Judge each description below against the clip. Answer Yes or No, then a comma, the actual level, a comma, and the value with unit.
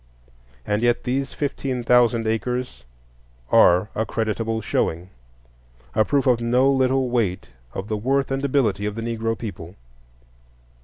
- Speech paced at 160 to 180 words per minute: No, slow, 135 wpm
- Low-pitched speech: Yes, low, 115 Hz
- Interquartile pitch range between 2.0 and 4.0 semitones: No, average, 4.4 semitones